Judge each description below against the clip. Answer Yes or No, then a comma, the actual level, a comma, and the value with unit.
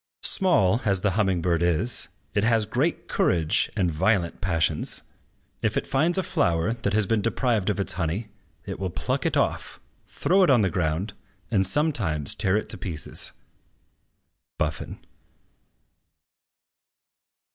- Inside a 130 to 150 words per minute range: Yes, average, 145 wpm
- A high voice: No, low, 100 Hz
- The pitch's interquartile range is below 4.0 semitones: No, average, 5.0 semitones